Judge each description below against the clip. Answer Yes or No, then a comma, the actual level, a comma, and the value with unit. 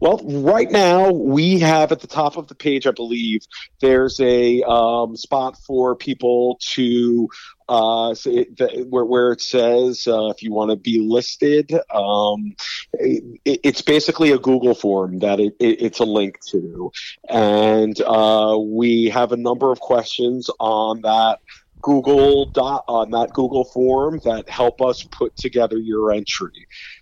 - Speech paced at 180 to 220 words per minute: No, average, 160 wpm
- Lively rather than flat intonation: No, average, 3.5 semitones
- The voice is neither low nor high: No, low, 120 Hz